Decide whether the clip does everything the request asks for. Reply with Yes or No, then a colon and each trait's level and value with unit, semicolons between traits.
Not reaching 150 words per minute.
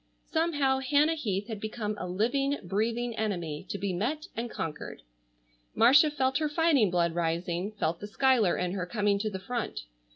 No: average, 170 wpm